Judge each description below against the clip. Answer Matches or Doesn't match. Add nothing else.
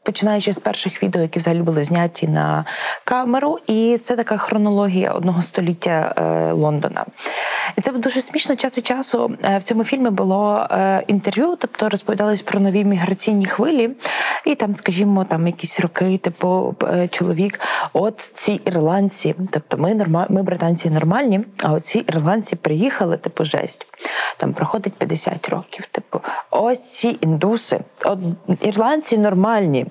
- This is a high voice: Matches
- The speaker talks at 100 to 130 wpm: Doesn't match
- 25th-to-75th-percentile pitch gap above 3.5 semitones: Matches